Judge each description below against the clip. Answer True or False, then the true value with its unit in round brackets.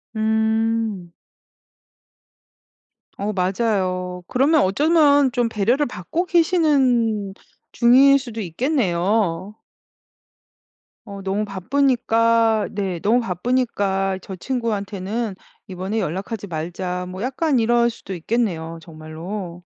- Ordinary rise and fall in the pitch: True (4.5 semitones)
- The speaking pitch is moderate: False (215 Hz)